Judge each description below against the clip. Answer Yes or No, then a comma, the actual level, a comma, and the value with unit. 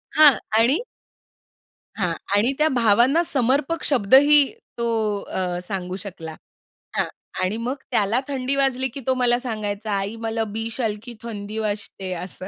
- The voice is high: Yes, high, 225 Hz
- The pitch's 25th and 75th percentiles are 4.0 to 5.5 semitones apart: Yes, average, 4.5 semitones